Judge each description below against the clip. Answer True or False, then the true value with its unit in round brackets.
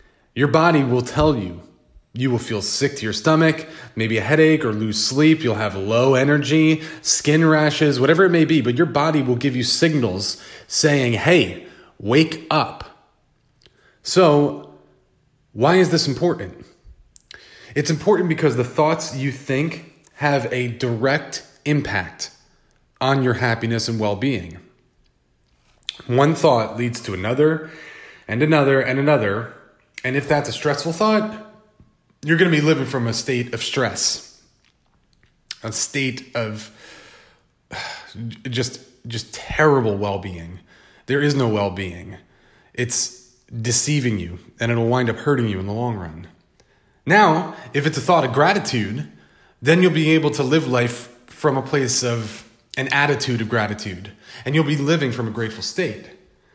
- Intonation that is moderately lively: True (4.9 semitones)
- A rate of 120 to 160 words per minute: True (150 wpm)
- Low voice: True (130 Hz)